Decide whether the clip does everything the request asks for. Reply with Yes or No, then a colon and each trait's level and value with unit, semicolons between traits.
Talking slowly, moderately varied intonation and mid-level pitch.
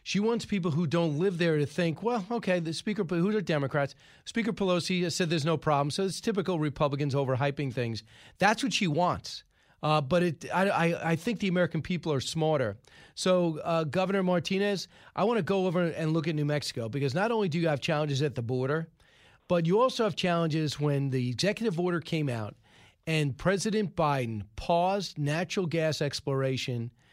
No: average, 190 wpm; average, 4.2 semitones; medium, 165 Hz